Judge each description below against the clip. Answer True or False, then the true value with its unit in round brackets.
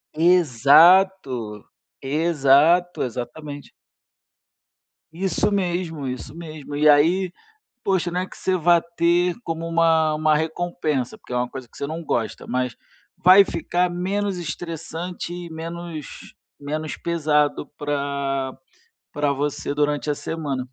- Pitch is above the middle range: False (160 Hz)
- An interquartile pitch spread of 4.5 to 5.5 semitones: False (3.4 semitones)